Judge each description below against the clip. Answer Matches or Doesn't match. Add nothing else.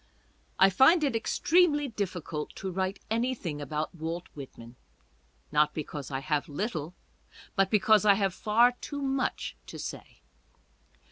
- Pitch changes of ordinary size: Doesn't match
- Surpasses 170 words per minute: Doesn't match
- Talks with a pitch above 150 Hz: Matches